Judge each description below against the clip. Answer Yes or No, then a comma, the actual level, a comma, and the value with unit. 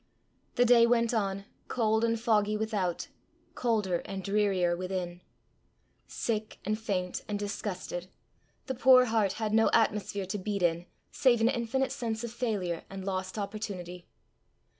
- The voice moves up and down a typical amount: Yes, average, 3.3 semitones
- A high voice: Yes, high, 210 Hz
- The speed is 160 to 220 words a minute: No, average, 140 wpm